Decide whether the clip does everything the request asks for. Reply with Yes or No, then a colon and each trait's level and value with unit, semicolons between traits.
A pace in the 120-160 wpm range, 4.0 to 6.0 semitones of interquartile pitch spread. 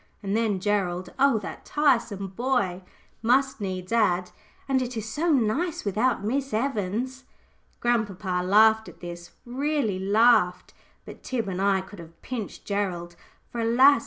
Yes: average, 145 wpm; average, 5.0 semitones